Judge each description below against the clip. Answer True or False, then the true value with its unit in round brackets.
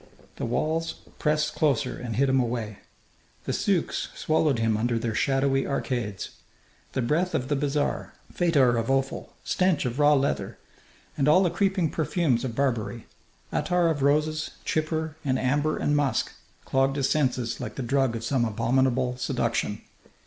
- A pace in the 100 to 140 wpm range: False (155 wpm)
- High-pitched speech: False (135 Hz)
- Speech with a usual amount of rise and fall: True (3.8 semitones)